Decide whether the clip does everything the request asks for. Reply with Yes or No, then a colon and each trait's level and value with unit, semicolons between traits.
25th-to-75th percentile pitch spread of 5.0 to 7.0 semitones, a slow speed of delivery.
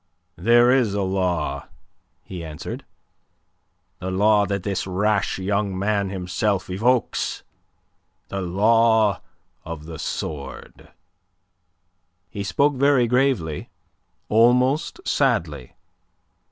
No: average, 4.0 semitones; slow, 95 wpm